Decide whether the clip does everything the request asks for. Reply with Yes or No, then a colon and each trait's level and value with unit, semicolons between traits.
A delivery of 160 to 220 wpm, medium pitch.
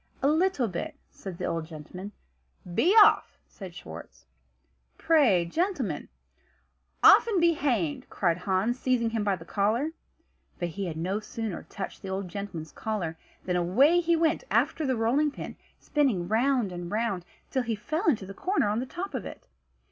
No: average, 175 wpm; high, 215 Hz